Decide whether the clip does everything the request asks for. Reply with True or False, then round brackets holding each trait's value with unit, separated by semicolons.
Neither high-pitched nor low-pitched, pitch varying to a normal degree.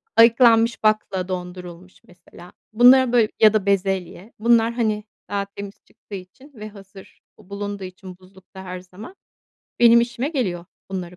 False (200 Hz; 3.9 semitones)